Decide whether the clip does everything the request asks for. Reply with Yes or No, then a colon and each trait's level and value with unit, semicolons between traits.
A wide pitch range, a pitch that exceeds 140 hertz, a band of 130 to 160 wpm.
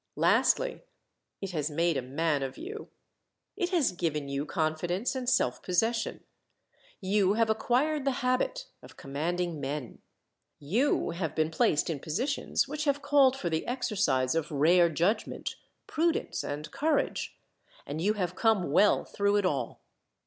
Yes: wide, 8.4 semitones; medium, 185 Hz; average, 150 wpm